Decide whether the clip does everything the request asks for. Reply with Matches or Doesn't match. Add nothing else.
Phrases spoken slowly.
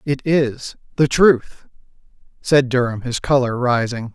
Matches